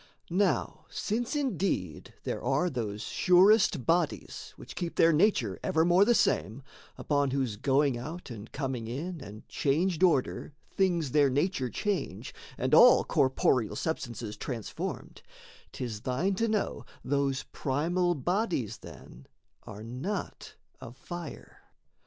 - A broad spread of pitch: Yes, wide, 6.3 semitones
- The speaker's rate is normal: No, slow, 125 wpm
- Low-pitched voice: No, medium, 145 Hz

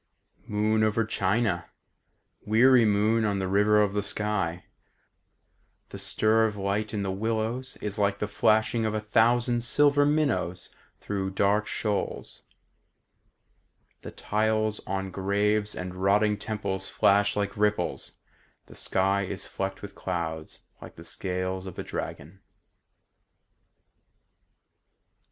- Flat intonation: Yes, narrow, 2.1 semitones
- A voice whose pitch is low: Yes, low, 105 Hz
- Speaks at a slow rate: Yes, slow, 125 wpm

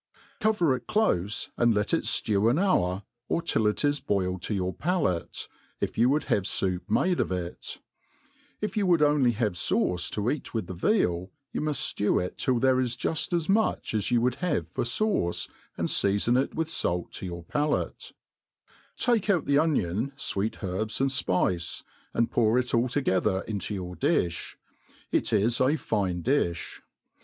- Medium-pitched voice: No, low, 115 Hz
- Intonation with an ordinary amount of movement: No, wide, 7.8 semitones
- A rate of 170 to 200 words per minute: Yes, average, 180 wpm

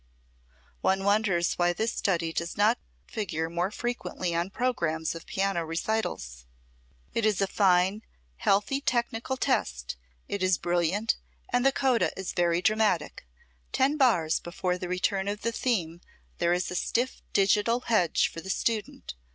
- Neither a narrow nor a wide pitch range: Yes, average, 4.4 semitones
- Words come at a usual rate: Yes, average, 150 wpm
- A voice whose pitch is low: No, high, 190 Hz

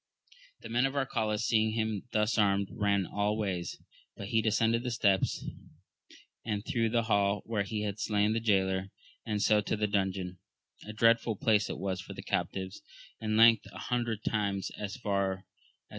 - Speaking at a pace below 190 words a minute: Yes, average, 180 wpm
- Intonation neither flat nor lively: No, narrow, 2.1 semitones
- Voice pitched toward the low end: Yes, low, 105 Hz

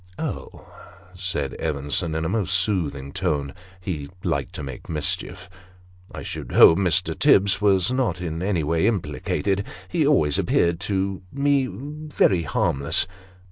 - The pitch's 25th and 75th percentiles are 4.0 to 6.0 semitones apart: Yes, average, 4.6 semitones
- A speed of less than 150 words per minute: Yes, average, 140 wpm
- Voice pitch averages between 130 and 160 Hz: No, very low, 90 Hz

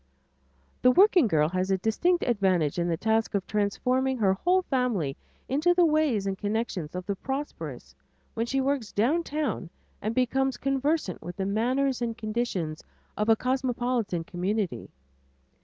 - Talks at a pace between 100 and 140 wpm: No, average, 155 wpm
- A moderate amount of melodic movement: No, wide, 5.8 semitones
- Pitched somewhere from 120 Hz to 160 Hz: No, high, 225 Hz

